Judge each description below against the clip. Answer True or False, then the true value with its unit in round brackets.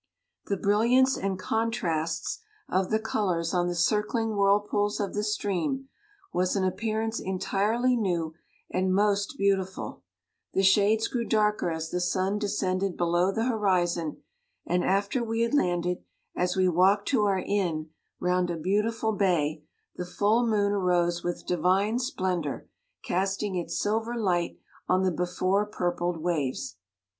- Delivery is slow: False (150 wpm)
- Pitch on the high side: True (195 Hz)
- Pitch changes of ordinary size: True (3.1 semitones)